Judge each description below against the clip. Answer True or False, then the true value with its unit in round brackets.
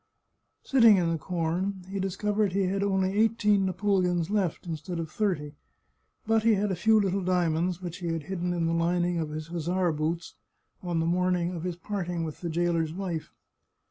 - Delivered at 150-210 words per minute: True (190 wpm)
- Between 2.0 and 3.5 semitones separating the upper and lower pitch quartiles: True (2.7 semitones)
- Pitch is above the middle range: False (180 Hz)